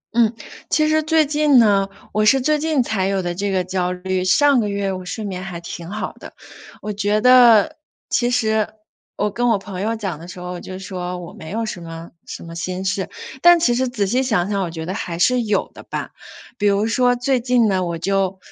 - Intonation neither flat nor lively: Yes, average, 4.7 semitones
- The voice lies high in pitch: Yes, high, 200 Hz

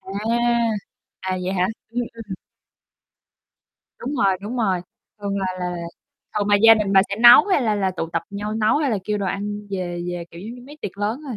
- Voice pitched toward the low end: No, high, 205 Hz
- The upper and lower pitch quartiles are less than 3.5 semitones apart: Yes, average, 3.1 semitones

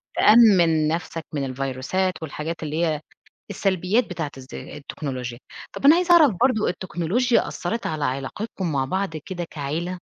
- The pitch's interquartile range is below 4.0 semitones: No, average, 5.3 semitones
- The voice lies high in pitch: No, medium, 170 Hz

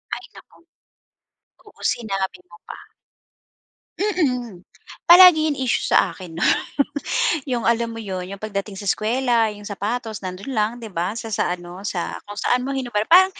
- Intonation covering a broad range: No, average, 4.1 semitones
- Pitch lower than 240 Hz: Yes, high, 220 Hz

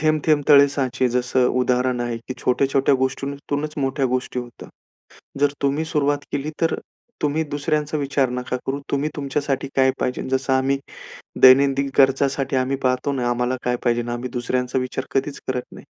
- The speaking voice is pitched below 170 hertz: Yes, low, 135 Hz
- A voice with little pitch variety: Yes, narrow, 2.0 semitones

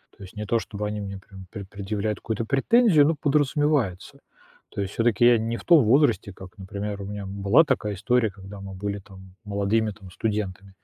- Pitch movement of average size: Yes, average, 3.0 semitones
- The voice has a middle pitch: No, low, 105 Hz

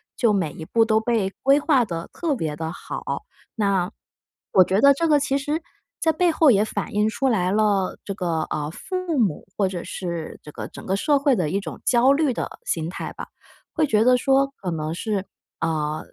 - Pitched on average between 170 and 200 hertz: No, high, 210 Hz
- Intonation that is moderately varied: No, wide, 7.5 semitones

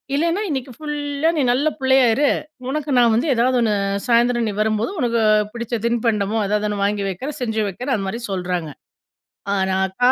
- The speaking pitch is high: Yes, high, 235 Hz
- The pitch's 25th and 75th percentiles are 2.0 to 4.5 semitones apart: Yes, average, 4.2 semitones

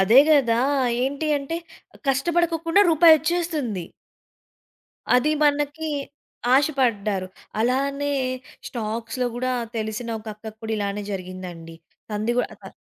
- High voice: Yes, very high, 250 Hz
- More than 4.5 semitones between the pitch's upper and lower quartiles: Yes, wide, 5.6 semitones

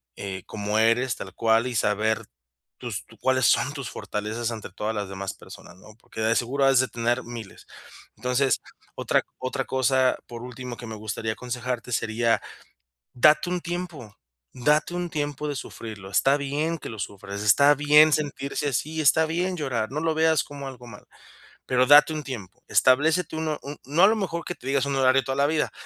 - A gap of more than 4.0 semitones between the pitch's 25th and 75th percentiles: Yes, average, 4.7 semitones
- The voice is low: Yes, low, 130 Hz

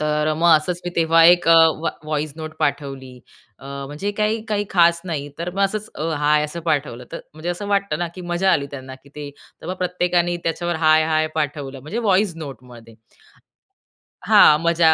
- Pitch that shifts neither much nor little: Yes, average, 3.1 semitones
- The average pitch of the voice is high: No, medium, 160 Hz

